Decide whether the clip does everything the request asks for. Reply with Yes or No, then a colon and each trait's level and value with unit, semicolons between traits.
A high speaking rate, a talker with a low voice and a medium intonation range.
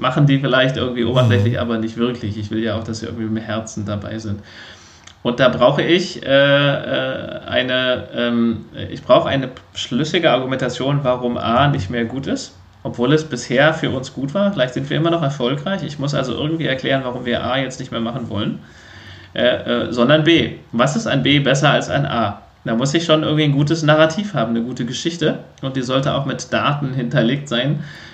Yes: fast, 205 wpm; low, 125 Hz; average, 3.7 semitones